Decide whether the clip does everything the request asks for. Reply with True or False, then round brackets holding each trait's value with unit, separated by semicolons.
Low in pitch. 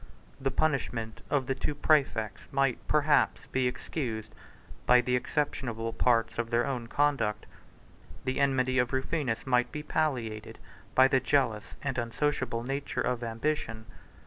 True (130 Hz)